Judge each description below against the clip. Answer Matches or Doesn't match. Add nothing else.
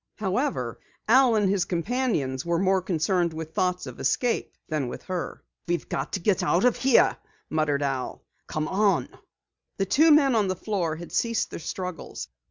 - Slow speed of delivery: Doesn't match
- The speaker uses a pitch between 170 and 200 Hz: Matches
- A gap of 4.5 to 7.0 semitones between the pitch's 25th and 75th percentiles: Matches